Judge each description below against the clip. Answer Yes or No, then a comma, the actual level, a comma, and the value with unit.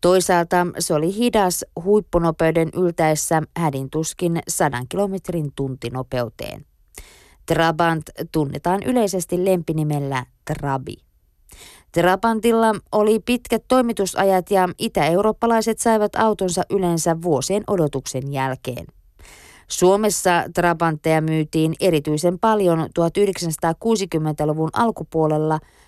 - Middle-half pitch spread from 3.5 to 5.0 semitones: Yes, average, 4.0 semitones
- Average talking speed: No, slow, 80 wpm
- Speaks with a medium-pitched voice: Yes, medium, 170 Hz